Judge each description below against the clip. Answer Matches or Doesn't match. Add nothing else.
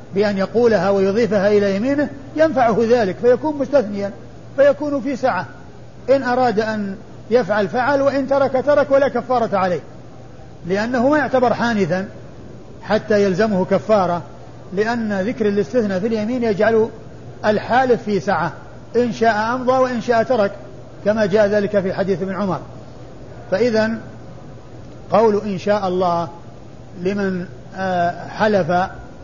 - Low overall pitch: Doesn't match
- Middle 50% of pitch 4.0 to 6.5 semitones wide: Matches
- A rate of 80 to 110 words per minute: Doesn't match